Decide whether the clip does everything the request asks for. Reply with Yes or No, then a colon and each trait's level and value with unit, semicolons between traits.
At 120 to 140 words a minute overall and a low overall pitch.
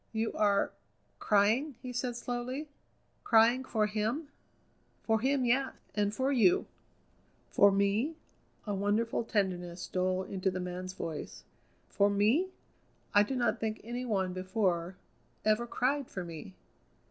No: slow, 135 wpm; high, 215 Hz